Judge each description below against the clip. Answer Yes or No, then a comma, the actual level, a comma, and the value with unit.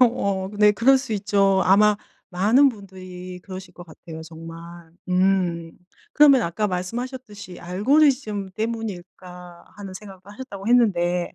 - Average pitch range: Yes, average, 3.5 semitones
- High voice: Yes, high, 195 Hz